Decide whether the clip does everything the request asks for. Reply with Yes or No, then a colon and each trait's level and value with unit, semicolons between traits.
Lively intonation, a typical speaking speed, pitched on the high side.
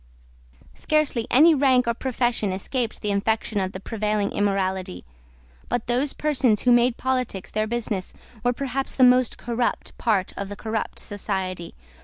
No: average, 3.9 semitones; average, 150 wpm; high, 225 Hz